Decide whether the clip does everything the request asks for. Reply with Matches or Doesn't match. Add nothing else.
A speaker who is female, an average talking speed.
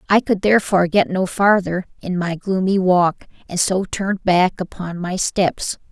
Matches